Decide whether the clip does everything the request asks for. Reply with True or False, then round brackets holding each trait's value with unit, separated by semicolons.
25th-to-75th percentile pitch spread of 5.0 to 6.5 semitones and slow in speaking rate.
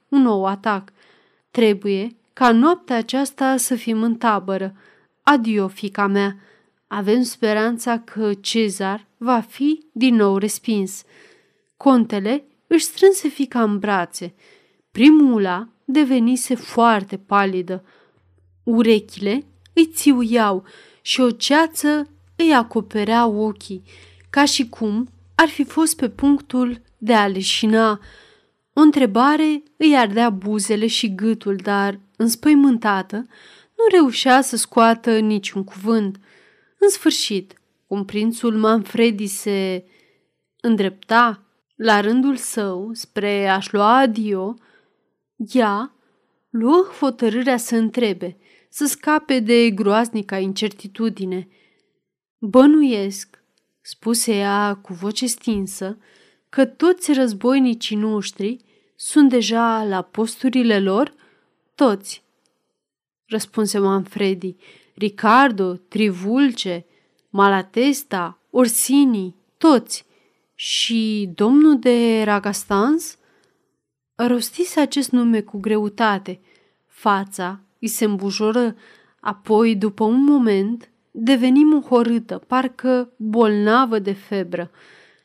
False (4.2 semitones; 95 wpm)